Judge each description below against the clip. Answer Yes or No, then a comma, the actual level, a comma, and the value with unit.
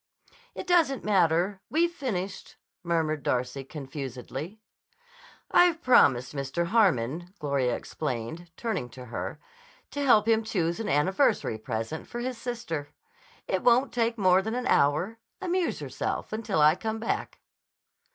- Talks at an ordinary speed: No, slow, 130 wpm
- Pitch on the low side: No, medium, 180 Hz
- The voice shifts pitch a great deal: Yes, wide, 8.5 semitones